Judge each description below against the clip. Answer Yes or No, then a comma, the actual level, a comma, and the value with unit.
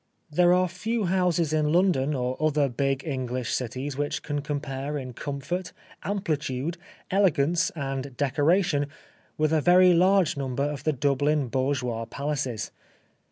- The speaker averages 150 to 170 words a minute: No, slow, 135 wpm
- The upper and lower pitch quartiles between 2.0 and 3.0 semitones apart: No, average, 4.1 semitones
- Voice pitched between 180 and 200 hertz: No, medium, 145 Hz